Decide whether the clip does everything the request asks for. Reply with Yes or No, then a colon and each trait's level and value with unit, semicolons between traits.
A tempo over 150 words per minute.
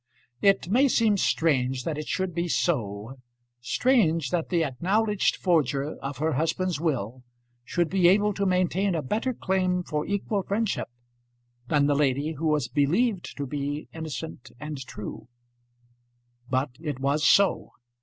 No: average, 145 wpm